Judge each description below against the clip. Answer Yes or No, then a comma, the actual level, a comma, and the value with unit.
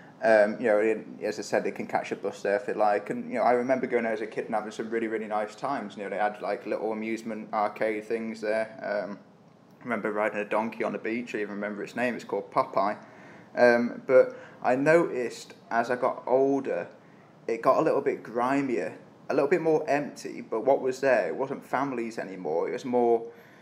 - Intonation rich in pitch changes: No, average, 3.6 semitones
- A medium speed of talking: No, fast, 225 wpm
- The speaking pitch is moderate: No, low, 115 Hz